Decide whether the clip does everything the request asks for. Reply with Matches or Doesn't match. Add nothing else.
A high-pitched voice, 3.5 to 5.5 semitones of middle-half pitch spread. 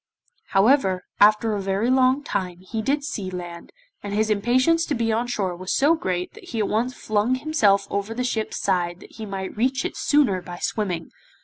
Matches